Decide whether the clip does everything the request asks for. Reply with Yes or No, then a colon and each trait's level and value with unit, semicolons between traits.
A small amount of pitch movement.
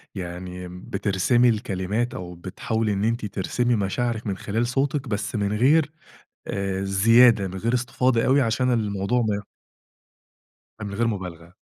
No: average, 4.0 semitones